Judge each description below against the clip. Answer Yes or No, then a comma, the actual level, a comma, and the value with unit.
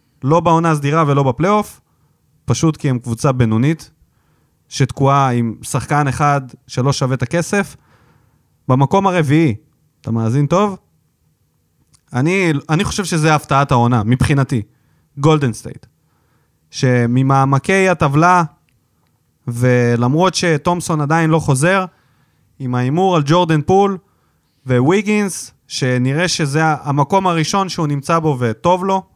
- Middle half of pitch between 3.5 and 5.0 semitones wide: Yes, average, 4.7 semitones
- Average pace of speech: Yes, average, 110 wpm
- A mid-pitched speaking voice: Yes, medium, 145 Hz